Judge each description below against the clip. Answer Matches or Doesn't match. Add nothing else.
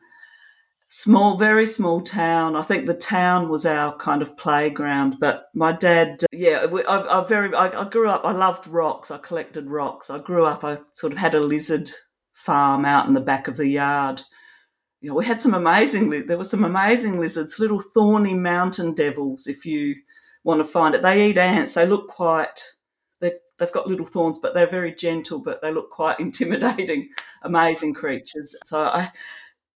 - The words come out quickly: Doesn't match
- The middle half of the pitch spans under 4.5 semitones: Doesn't match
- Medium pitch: Matches